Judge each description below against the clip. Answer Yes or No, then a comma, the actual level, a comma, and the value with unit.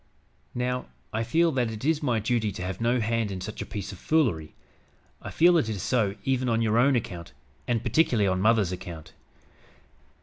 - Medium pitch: No, low, 115 Hz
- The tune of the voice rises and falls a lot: No, average, 4.1 semitones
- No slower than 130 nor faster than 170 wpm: No, average, 195 wpm